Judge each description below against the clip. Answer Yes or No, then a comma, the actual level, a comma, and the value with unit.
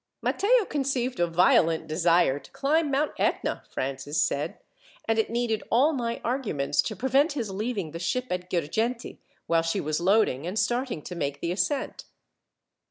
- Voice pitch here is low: No, high, 210 Hz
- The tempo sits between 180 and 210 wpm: No, average, 165 wpm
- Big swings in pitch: Yes, wide, 7.3 semitones